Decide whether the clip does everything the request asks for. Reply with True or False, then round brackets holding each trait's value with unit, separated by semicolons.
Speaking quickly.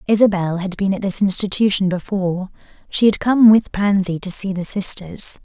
False (175 wpm)